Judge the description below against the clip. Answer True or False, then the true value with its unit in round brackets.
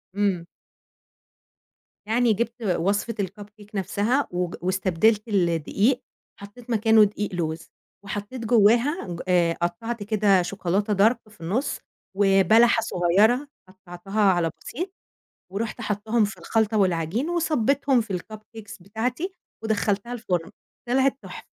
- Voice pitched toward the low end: False (210 Hz)